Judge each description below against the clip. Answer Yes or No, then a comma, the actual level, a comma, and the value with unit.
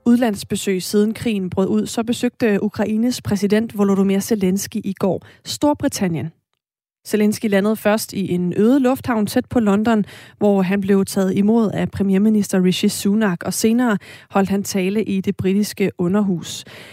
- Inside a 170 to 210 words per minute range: No, average, 150 wpm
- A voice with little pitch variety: Yes, narrow, 2.3 semitones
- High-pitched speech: Yes, high, 205 Hz